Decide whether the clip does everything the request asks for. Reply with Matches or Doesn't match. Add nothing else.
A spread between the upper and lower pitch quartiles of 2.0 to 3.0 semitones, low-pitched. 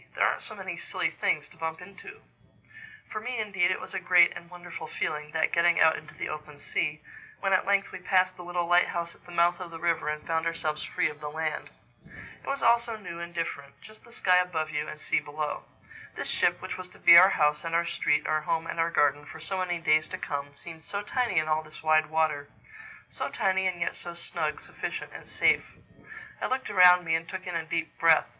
Doesn't match